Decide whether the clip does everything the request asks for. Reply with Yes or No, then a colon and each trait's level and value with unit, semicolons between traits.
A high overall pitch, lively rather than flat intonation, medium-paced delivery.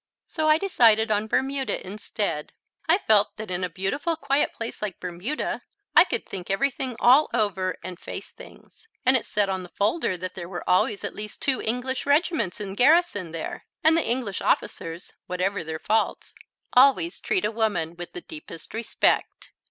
Yes: high, 215 Hz; wide, 6.5 semitones; average, 175 wpm